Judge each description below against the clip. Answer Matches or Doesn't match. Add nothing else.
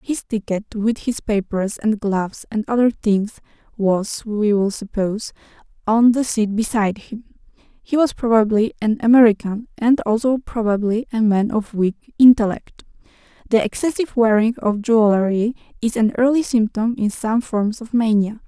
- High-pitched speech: Matches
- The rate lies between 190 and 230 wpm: Doesn't match